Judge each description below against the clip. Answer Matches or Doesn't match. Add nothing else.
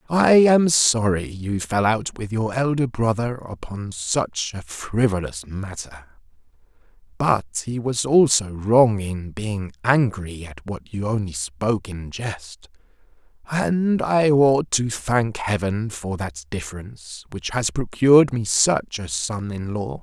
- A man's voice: Matches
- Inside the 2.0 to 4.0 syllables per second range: Matches